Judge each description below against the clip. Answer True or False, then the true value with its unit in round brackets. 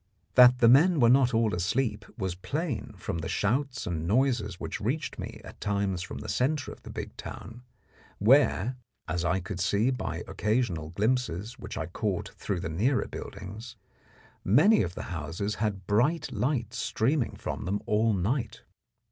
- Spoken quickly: False (165 wpm)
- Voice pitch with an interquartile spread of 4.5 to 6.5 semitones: True (5.1 semitones)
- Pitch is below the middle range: True (110 Hz)